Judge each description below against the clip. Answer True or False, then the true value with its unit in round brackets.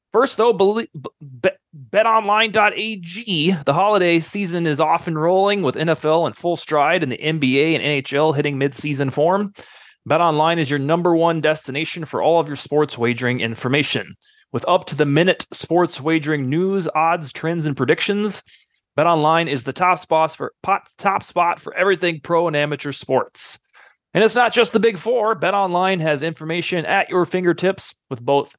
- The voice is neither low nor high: True (165 Hz)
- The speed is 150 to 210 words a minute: True (160 wpm)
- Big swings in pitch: False (4.1 semitones)